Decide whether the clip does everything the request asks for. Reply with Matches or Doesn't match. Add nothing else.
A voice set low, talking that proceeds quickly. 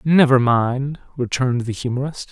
Doesn't match